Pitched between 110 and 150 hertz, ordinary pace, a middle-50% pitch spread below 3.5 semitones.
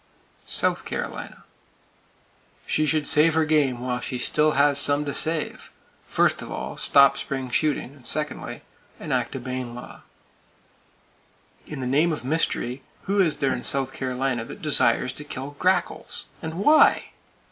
Yes: medium, 140 Hz; average, 145 wpm; average, 3.1 semitones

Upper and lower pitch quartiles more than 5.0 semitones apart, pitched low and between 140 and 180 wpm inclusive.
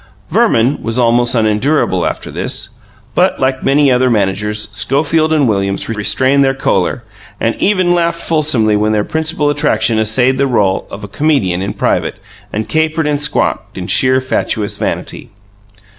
Yes: wide, 5.6 semitones; low, 125 Hz; average, 160 wpm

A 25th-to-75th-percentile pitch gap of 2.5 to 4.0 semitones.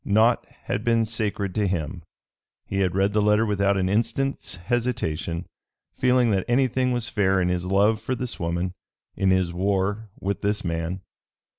Yes: average, 3.4 semitones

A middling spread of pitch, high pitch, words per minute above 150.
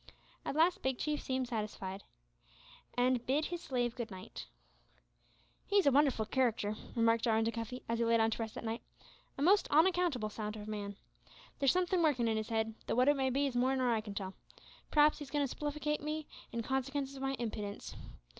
Yes: average, 4.5 semitones; very high, 250 Hz; average, 200 wpm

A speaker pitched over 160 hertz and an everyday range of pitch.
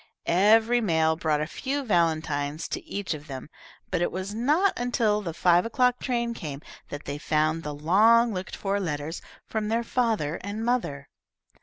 No: medium, 185 Hz; wide, 6.8 semitones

